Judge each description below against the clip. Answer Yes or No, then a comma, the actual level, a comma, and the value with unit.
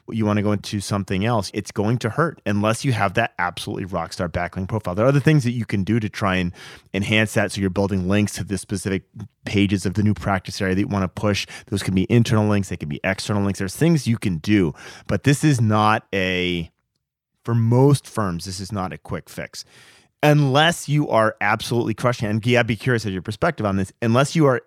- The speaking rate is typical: No, fast, 235 wpm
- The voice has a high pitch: No, low, 105 Hz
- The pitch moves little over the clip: No, average, 3.3 semitones